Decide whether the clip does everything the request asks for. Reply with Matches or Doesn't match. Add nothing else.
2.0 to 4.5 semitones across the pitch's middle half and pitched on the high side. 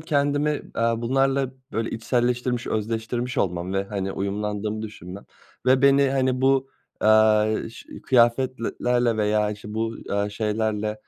Doesn't match